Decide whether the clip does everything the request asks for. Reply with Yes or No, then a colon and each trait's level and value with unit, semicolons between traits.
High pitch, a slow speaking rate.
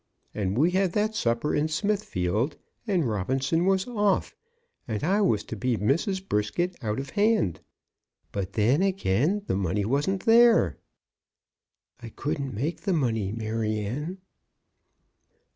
No: medium, 140 Hz; slow, 130 wpm